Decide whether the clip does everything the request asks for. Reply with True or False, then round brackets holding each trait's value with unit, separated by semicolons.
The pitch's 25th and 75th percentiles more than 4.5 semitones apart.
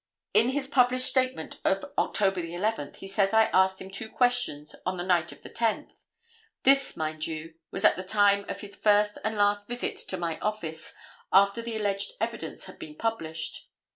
False (4.1 semitones)